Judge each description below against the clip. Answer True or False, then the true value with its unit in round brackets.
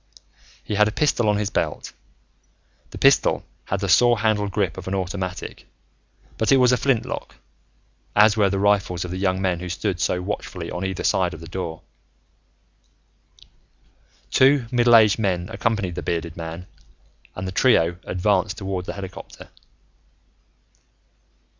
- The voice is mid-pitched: False (95 Hz)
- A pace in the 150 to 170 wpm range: True (155 wpm)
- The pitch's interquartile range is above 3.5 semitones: False (3.0 semitones)